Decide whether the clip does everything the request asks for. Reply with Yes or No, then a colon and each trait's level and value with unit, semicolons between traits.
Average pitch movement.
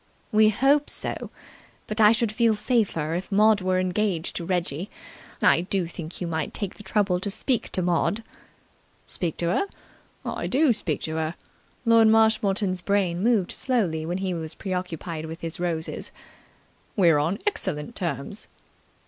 Yes: average, 4.2 semitones